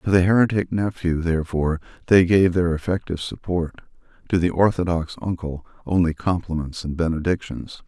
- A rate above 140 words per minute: No, slow, 135 wpm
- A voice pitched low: Yes, very low, 85 Hz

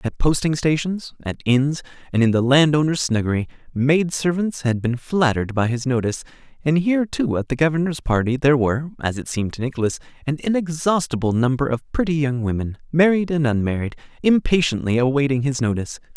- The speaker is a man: Yes, male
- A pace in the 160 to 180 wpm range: Yes, average, 165 wpm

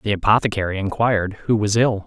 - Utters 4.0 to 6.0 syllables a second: No, 6.2 syllables/s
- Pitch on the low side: Yes, low, 105 Hz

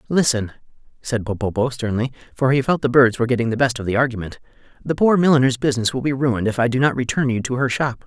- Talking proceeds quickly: Yes, fast, 240 wpm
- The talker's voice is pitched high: No, low, 125 Hz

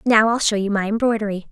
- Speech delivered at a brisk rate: Yes, fast, 235 wpm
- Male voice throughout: No, female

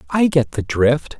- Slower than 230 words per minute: Yes, average, 200 wpm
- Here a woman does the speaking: No, male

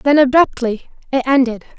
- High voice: Yes, very high, 260 Hz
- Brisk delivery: No, slow, 135 wpm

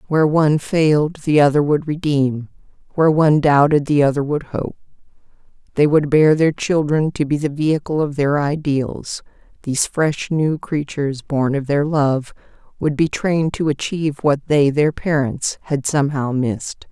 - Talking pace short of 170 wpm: Yes, average, 160 wpm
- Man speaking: No, female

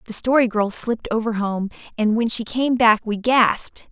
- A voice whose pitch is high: Yes, high, 230 Hz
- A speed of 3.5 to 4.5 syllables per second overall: No, 4.9 syllables/s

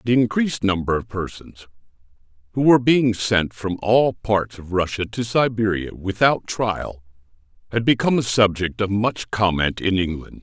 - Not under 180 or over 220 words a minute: No, average, 155 wpm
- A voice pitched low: Yes, low, 105 Hz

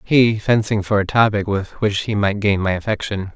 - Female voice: No, male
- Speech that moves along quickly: Yes, fast, 215 wpm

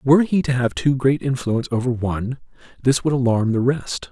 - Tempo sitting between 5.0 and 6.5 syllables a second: Yes, 5.6 syllables/s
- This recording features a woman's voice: No, male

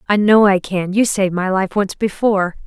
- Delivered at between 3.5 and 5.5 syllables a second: Yes, 5.4 syllables/s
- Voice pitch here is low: No, high, 195 Hz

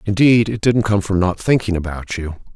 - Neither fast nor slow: No, fast, 210 wpm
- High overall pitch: No, low, 100 Hz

